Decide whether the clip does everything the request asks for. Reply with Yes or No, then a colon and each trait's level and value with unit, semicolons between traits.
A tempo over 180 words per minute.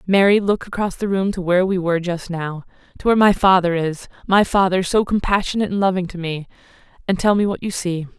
Yes: average, 200 wpm